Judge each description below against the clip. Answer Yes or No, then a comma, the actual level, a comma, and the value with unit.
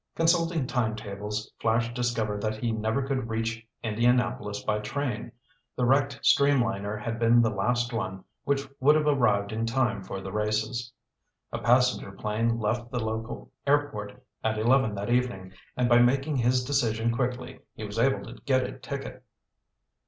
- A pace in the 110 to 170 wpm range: Yes, average, 160 wpm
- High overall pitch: No, low, 115 Hz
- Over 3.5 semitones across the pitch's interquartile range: No, average, 2.7 semitones